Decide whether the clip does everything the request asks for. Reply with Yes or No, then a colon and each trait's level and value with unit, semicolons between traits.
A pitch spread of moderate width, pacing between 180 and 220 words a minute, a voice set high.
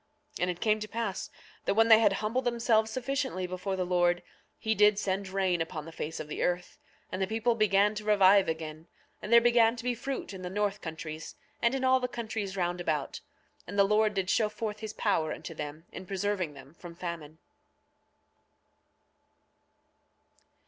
Yes: average, 3.9 semitones; average, 190 wpm; high, 200 Hz